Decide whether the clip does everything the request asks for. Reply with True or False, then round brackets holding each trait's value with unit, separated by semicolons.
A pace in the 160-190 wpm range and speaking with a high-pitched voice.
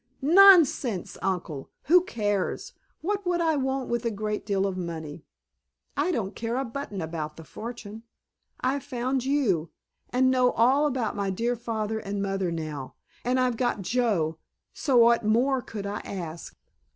False (150 wpm; 230 Hz)